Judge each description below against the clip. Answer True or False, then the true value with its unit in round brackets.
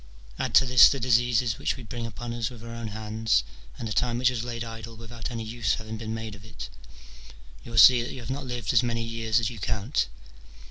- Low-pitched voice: True (115 Hz)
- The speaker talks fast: True (240 wpm)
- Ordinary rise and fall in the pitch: False (1.6 semitones)